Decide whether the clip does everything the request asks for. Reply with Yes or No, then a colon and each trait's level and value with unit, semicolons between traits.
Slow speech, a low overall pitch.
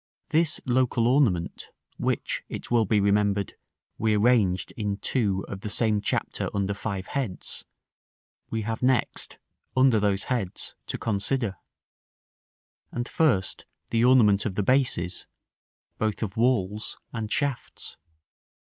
Yes: slow, 130 wpm; low, 110 Hz